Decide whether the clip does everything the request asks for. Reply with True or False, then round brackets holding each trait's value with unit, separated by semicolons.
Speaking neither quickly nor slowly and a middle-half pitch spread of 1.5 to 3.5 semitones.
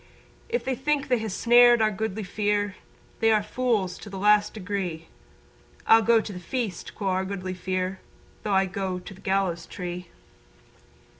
True (170 wpm; 3.0 semitones)